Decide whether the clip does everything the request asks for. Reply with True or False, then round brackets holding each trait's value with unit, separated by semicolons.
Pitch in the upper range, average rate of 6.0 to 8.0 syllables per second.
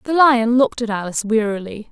True (230 Hz; 6.3 syllables/s)